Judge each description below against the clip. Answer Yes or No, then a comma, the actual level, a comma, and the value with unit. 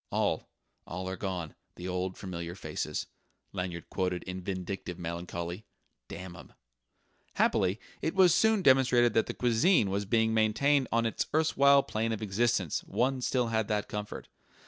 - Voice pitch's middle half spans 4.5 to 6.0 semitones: Yes, average, 4.9 semitones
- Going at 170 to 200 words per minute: No, average, 150 wpm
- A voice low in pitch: Yes, low, 105 Hz